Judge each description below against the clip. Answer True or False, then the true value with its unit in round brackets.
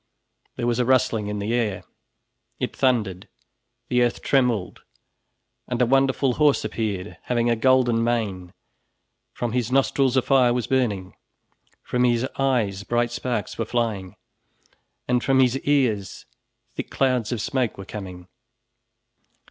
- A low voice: True (120 Hz)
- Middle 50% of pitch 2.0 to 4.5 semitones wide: True (3.4 semitones)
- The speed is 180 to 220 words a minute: False (140 wpm)